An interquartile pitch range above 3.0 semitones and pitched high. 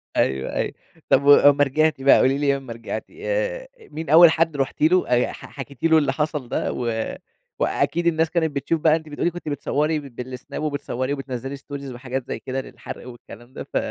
No: average, 3.5 semitones; medium, 145 Hz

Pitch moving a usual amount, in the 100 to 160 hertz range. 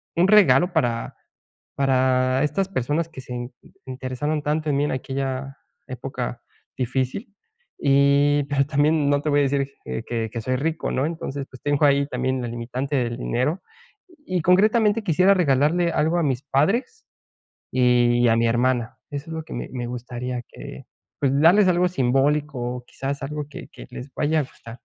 Yes: average, 3.6 semitones; medium, 140 Hz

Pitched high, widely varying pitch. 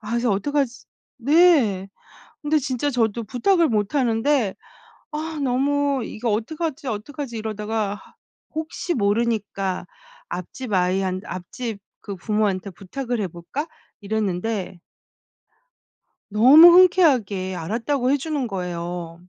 Yes: high, 225 Hz; wide, 6.2 semitones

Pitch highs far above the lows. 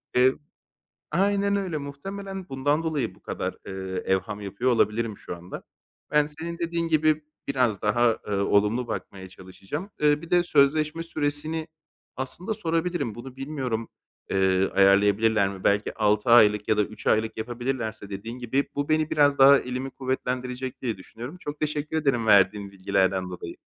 Yes: wide, 6.5 semitones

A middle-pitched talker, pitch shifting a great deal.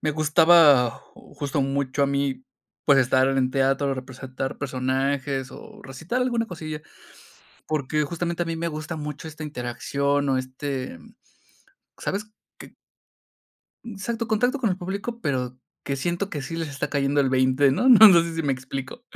No: medium, 145 Hz; average, 4.2 semitones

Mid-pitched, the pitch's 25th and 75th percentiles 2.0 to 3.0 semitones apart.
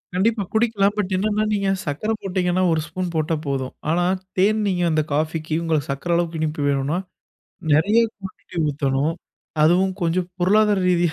No: medium, 175 Hz; average, 4.0 semitones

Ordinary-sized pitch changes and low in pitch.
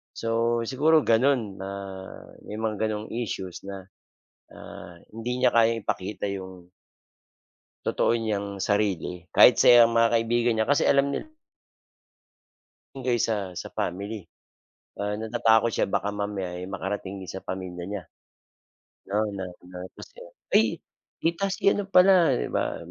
Yes: average, 3.5 semitones; low, 110 Hz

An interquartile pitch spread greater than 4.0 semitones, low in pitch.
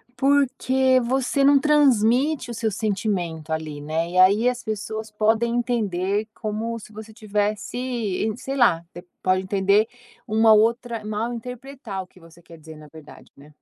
No: average, 4.5 semitones; high, 220 Hz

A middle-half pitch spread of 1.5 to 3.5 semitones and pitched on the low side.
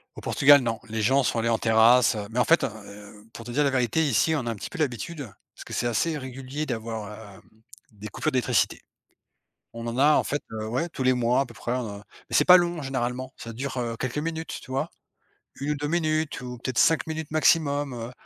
No: average, 4.2 semitones; low, 130 Hz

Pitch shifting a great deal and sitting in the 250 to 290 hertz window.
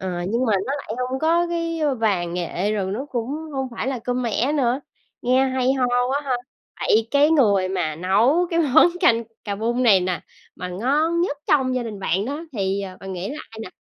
No: wide, 5.8 semitones; high, 240 Hz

